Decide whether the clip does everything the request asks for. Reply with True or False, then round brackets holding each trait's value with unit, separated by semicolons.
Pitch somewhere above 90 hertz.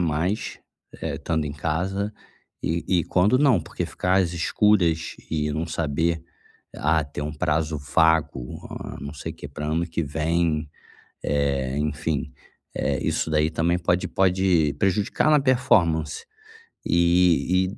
False (80 Hz)